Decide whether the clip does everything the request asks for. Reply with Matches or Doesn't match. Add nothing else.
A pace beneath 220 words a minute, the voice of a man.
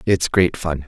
Matches